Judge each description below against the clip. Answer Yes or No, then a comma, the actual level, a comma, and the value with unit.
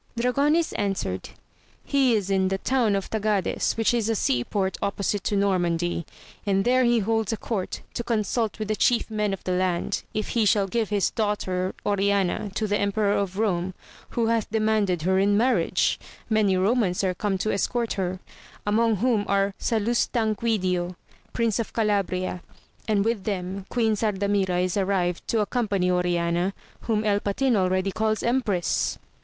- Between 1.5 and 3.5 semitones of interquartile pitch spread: Yes, average, 2.9 semitones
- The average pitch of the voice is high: Yes, high, 205 Hz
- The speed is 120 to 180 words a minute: Yes, average, 165 wpm